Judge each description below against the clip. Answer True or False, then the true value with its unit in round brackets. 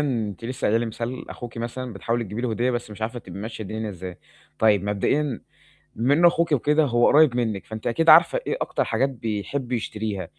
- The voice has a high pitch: False (115 Hz)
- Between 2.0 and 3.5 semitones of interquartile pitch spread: True (3.2 semitones)